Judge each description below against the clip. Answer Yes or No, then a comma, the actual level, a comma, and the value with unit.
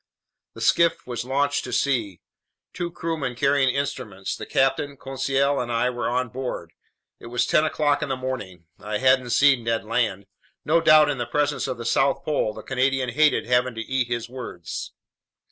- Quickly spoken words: No, average, 180 wpm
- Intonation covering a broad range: No, average, 3.0 semitones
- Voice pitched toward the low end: Yes, low, 130 Hz